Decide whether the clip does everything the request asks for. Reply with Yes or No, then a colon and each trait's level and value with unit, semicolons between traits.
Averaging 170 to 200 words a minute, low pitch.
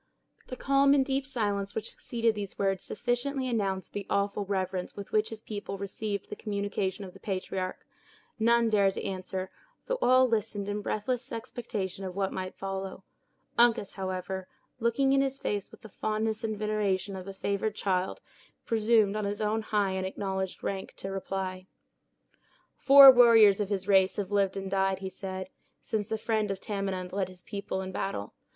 No: average, 175 wpm; high, 200 Hz